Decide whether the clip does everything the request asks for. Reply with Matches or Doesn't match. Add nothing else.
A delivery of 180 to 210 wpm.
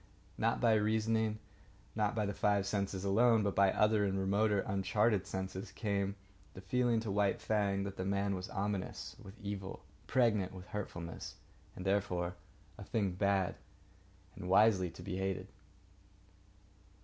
Doesn't match